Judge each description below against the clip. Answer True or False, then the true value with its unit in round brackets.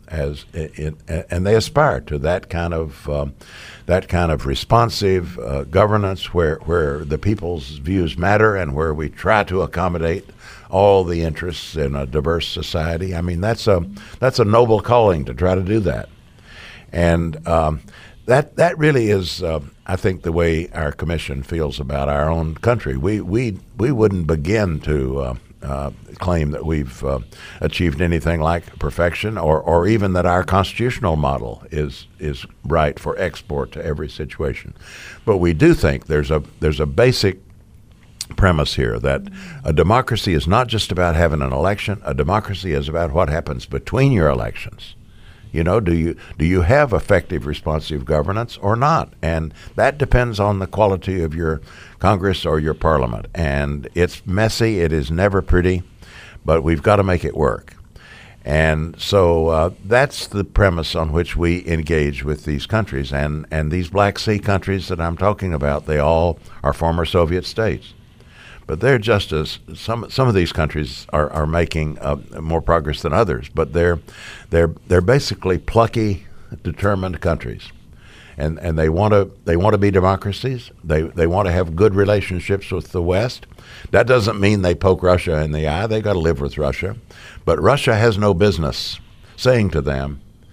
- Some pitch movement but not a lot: True (4.6 semitones)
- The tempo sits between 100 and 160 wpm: False (175 wpm)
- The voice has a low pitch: True (85 Hz)